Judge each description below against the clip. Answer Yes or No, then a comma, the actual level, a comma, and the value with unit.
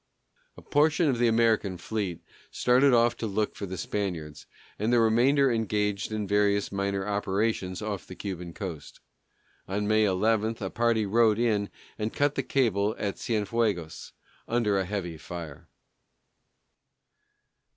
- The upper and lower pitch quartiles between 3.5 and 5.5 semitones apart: No, average, 2.9 semitones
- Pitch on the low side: Yes, low, 105 Hz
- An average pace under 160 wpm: Yes, average, 140 wpm